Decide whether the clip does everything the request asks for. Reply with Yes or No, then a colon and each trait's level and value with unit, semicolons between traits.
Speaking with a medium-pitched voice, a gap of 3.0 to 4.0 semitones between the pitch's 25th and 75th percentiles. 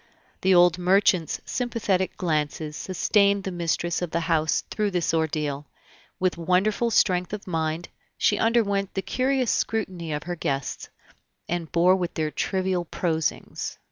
Yes: medium, 180 Hz; average, 3.4 semitones